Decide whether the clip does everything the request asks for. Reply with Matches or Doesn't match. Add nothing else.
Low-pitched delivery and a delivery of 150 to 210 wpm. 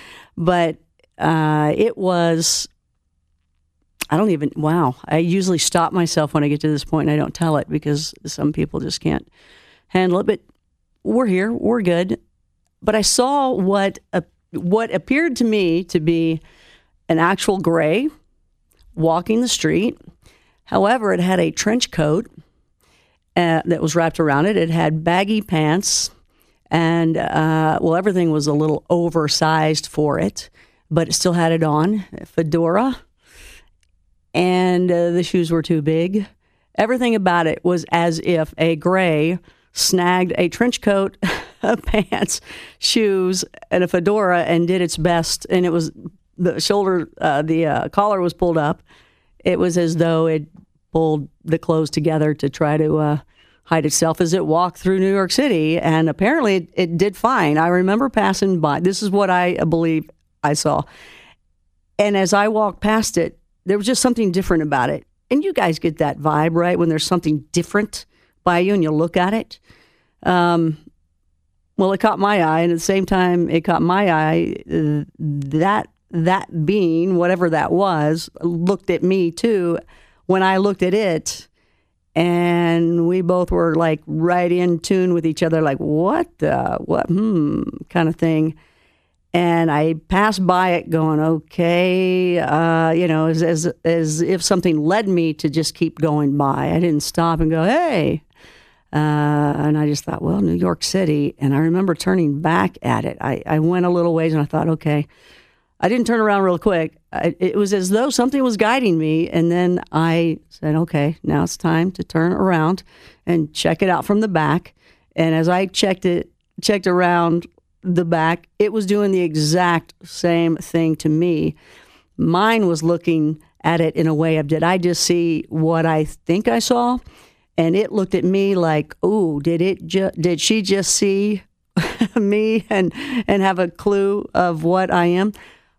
Doesn't match